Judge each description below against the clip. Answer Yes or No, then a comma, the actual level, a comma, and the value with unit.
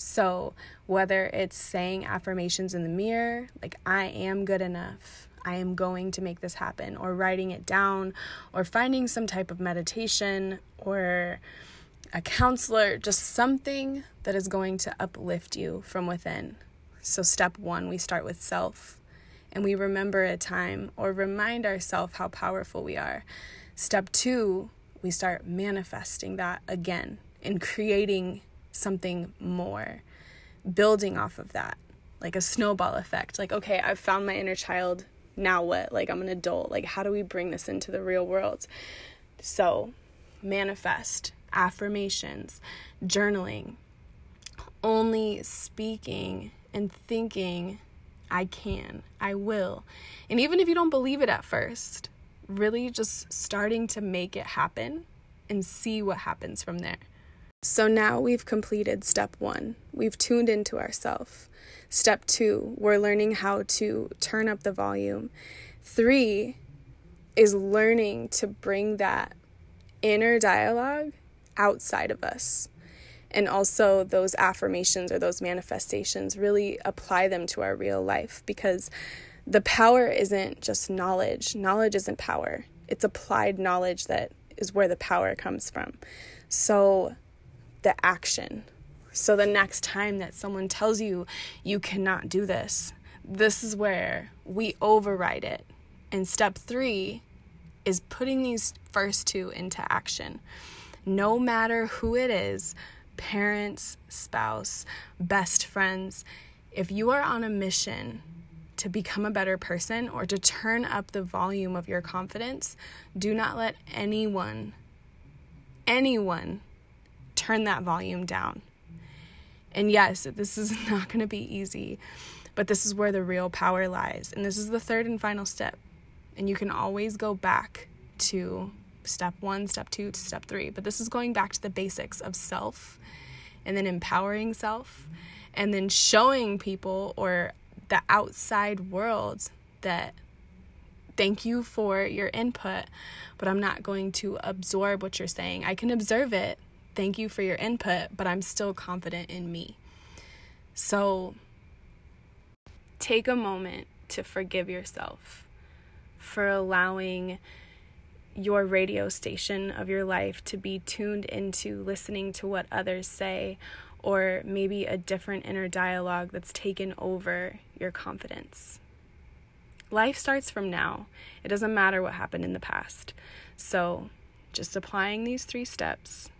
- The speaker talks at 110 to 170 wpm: Yes, average, 140 wpm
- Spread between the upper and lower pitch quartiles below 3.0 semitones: Yes, narrow, 2.6 semitones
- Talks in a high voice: Yes, high, 195 Hz